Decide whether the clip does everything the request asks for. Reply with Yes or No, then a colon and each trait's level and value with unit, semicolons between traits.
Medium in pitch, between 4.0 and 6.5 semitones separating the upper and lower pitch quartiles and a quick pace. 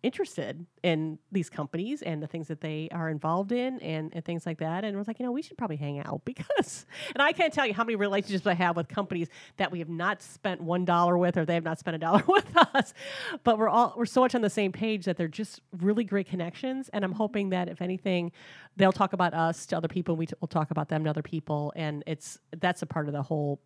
Yes: medium, 175 Hz; average, 4.3 semitones; fast, 265 wpm